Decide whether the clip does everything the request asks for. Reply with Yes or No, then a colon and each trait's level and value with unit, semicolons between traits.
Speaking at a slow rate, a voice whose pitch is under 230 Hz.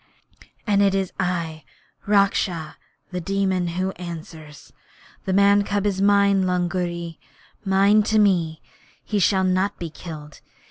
Yes: slow, 130 wpm; medium, 185 Hz